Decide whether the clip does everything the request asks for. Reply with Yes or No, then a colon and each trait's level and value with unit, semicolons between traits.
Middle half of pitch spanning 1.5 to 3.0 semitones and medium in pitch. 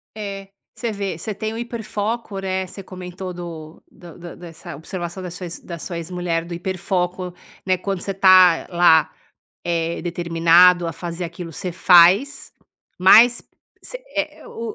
Yes: narrow, 2.4 semitones; medium, 180 Hz